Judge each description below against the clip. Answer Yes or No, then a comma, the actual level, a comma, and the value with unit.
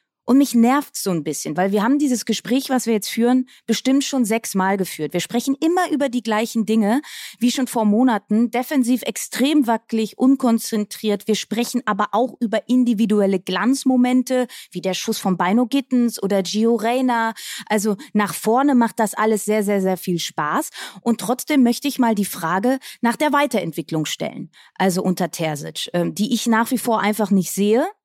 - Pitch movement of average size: Yes, average, 3.6 semitones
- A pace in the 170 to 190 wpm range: Yes, average, 180 wpm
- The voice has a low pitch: No, high, 230 Hz